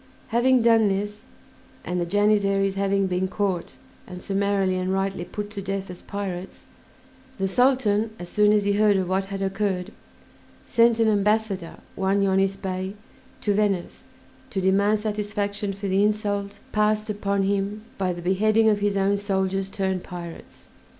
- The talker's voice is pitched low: No, high, 200 Hz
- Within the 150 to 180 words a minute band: Yes, average, 155 wpm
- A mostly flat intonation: Yes, narrow, 1.5 semitones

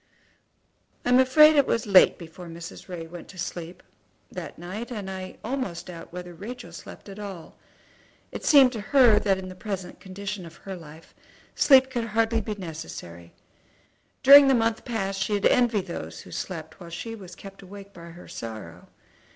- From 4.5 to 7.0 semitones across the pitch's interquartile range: Yes, average, 4.9 semitones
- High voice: Yes, high, 195 Hz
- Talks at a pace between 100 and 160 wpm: No, average, 185 wpm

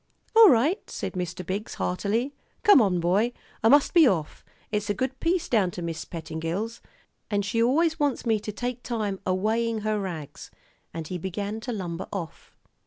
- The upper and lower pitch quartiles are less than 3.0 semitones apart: No, average, 5.0 semitones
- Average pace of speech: Yes, average, 180 wpm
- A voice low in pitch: No, high, 210 Hz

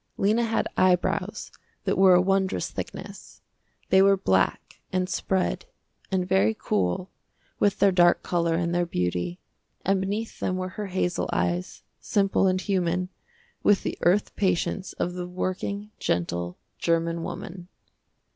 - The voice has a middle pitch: Yes, medium, 180 Hz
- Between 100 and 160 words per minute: Yes, average, 140 wpm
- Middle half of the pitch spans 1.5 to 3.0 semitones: Yes, narrow, 2.4 semitones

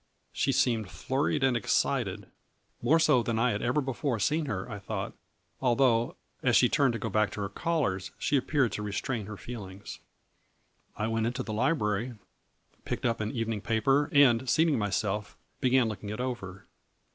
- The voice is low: Yes, low, 115 Hz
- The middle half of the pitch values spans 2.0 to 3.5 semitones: No, average, 3.9 semitones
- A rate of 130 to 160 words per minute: No, average, 170 wpm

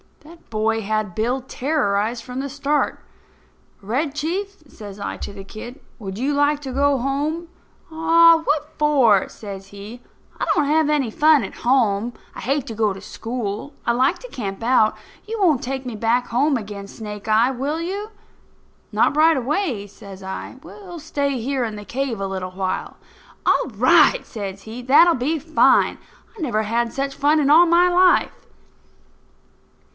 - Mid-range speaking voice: No, very high, 255 Hz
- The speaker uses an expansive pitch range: Yes, wide, 5.8 semitones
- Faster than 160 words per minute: Yes, average, 170 wpm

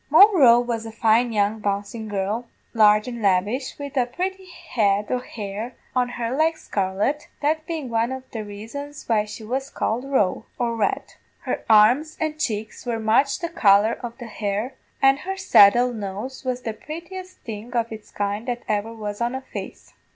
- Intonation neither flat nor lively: Yes, average, 4.2 semitones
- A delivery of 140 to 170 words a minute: No, average, 185 wpm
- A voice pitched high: Yes, high, 235 Hz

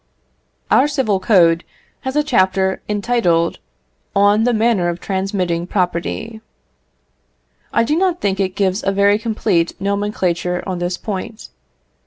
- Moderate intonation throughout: Yes, average, 3.7 semitones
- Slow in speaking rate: Yes, slow, 130 wpm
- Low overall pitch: No, high, 200 Hz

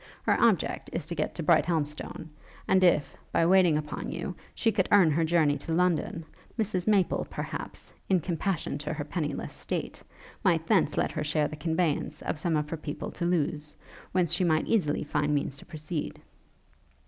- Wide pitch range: No, average, 3.0 semitones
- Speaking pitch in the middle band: Yes, medium, 160 Hz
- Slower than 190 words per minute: Yes, average, 180 wpm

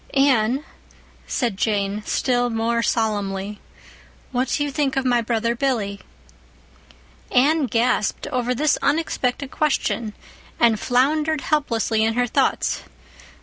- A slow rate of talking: Yes, slow, 115 wpm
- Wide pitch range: No, average, 3.5 semitones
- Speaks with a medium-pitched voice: No, high, 245 Hz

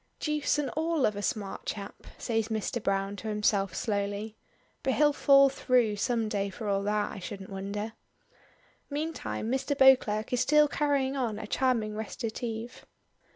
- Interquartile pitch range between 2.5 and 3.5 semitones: No, average, 4.4 semitones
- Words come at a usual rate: Yes, average, 155 wpm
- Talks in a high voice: Yes, high, 225 Hz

